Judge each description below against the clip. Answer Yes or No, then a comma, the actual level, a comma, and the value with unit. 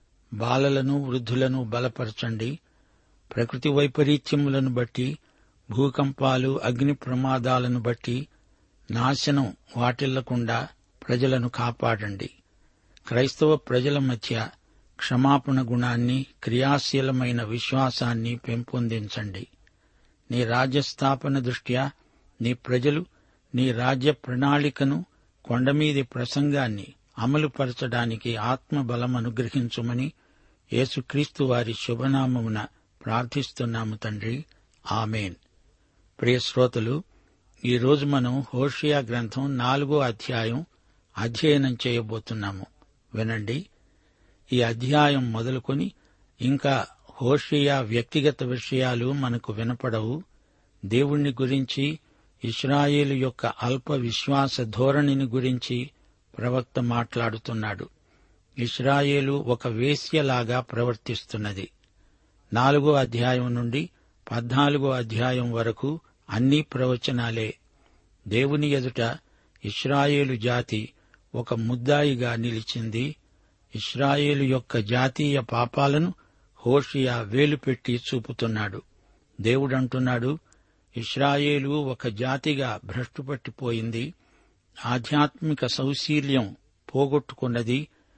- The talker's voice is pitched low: Yes, low, 125 Hz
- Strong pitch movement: No, average, 3.2 semitones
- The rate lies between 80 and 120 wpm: No, slow, 70 wpm